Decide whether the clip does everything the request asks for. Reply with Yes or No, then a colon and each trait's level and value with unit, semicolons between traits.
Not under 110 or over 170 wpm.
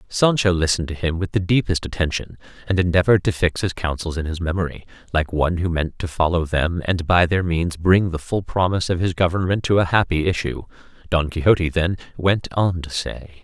No: fast, 205 wpm